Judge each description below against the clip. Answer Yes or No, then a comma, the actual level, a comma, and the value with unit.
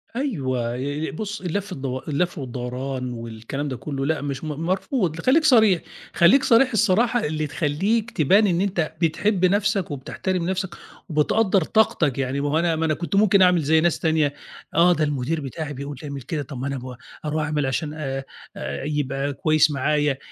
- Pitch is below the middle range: No, medium, 155 Hz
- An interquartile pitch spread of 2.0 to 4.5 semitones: No, average, 5.2 semitones